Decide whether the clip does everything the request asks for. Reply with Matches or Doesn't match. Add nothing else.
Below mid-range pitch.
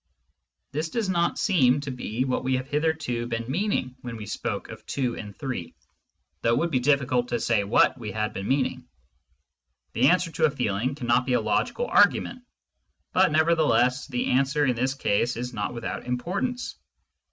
Matches